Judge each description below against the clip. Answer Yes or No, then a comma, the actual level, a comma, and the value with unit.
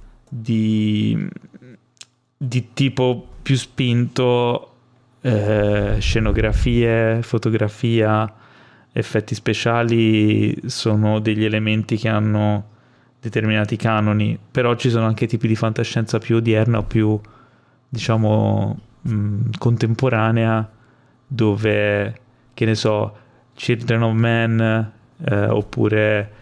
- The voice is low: Yes, low, 115 Hz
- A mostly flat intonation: Yes, narrow, 2.0 semitones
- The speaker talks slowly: Yes, slow, 90 wpm